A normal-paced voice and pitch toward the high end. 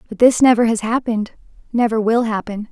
Yes: average, 155 wpm; high, 225 Hz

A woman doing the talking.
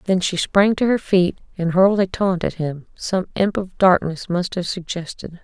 Yes: female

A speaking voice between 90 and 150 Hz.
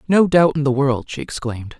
Yes: medium, 140 Hz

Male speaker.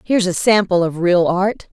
No: female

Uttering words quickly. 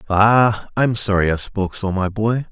No: average, 190 wpm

